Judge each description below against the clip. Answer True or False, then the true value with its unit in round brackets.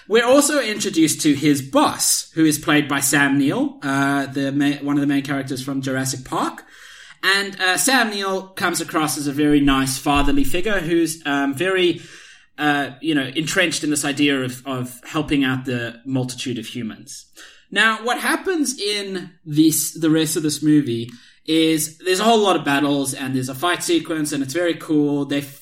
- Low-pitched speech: False (150 Hz)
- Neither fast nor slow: True (190 wpm)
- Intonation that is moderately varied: True (4.1 semitones)